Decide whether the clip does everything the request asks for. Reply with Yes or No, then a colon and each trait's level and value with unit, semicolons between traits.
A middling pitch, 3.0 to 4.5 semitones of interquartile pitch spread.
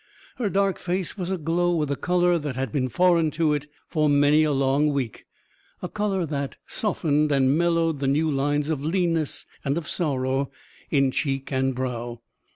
Yes: medium, 150 Hz; average, 3.9 semitones